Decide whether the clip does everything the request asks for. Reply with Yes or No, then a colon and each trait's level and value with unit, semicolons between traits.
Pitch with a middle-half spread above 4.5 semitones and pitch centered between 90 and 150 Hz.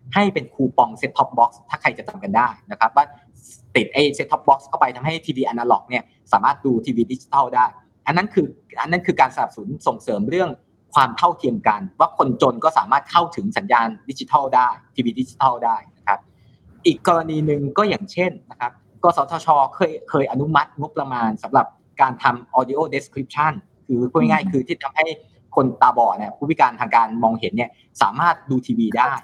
Yes: wide, 5.4 semitones; medium, 140 Hz